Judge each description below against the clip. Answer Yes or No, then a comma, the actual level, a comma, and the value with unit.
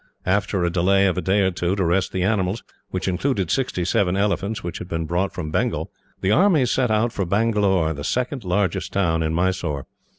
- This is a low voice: Yes, very low, 95 Hz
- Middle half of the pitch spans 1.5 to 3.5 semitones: Yes, average, 2.8 semitones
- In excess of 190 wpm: Yes, fast, 205 wpm